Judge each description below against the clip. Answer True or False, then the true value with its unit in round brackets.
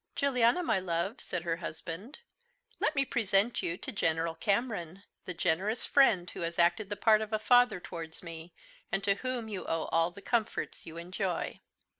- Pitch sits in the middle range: False (195 Hz)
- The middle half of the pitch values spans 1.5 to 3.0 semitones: False (5.0 semitones)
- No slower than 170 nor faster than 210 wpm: True (180 wpm)